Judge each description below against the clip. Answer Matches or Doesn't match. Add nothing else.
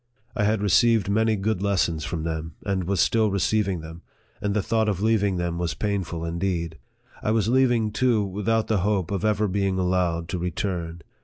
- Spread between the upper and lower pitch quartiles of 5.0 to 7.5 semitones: Doesn't match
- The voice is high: Doesn't match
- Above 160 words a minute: Matches